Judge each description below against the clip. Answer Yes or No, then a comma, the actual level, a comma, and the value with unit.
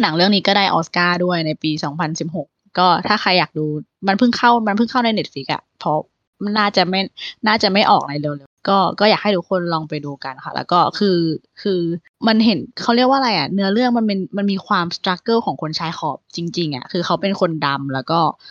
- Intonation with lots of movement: No, average, 4.3 semitones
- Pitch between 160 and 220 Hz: Yes, medium, 185 Hz